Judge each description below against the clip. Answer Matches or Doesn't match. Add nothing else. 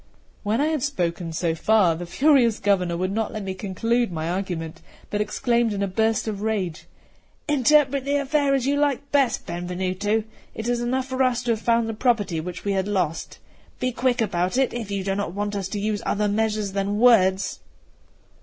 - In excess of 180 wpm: Matches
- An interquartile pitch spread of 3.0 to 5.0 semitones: Matches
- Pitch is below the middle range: Doesn't match